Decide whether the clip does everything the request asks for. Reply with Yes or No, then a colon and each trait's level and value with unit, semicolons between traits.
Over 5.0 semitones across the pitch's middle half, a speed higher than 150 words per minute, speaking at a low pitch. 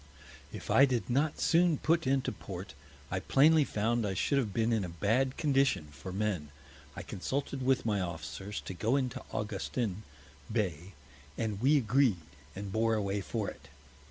Yes: wide, 5.5 semitones; average, 165 wpm; low, 110 Hz